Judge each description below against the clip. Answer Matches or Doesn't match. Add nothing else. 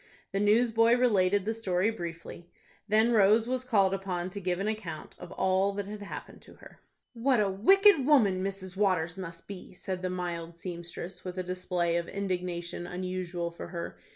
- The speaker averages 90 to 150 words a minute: Doesn't match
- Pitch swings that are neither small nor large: Matches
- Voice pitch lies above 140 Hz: Matches